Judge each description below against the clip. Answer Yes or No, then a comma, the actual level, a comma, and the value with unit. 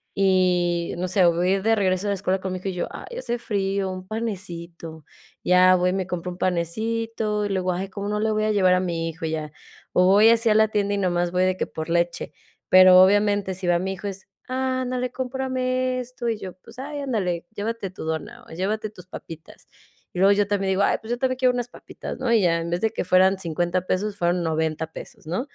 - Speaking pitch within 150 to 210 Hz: Yes, high, 190 Hz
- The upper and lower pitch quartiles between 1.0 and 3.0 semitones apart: No, average, 3.5 semitones